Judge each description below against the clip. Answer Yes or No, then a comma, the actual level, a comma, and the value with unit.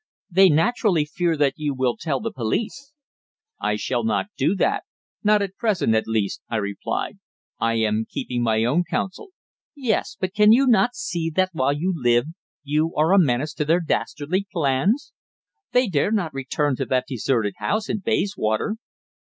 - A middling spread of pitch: No, wide, 7.7 semitones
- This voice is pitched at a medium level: Yes, medium, 160 Hz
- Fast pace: No, average, 170 wpm